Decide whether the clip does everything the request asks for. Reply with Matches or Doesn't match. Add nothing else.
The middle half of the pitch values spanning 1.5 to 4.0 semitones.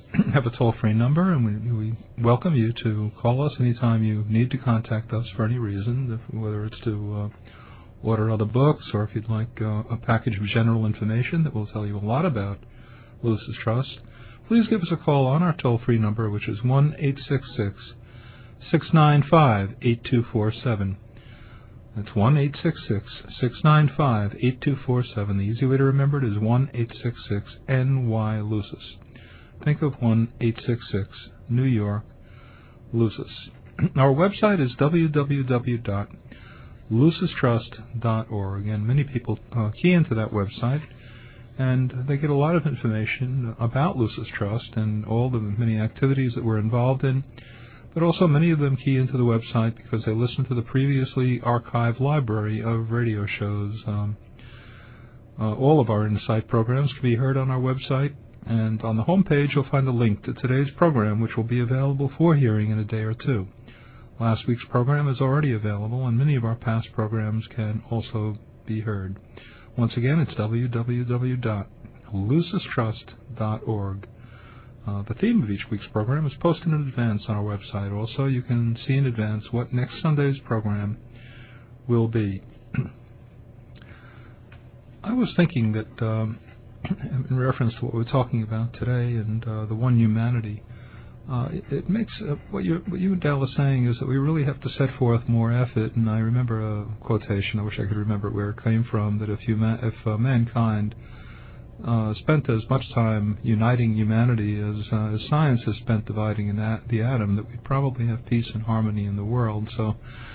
Matches